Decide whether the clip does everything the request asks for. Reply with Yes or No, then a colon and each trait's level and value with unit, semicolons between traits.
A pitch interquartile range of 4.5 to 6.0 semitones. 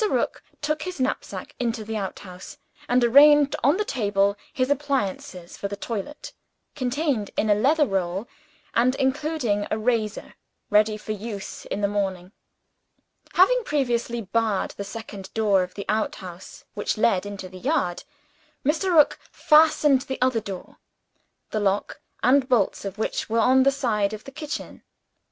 Yes: average, 5.2 semitones